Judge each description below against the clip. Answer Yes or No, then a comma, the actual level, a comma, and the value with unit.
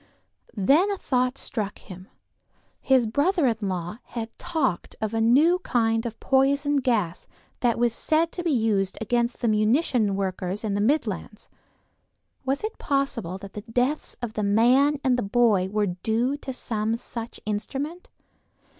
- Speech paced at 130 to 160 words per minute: Yes, average, 155 wpm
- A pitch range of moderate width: Yes, average, 4.5 semitones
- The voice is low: No, high, 235 Hz